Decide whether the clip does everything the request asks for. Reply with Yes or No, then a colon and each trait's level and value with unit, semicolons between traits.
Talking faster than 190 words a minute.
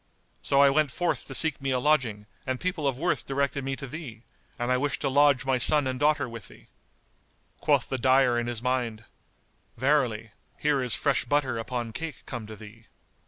Yes: average, 200 wpm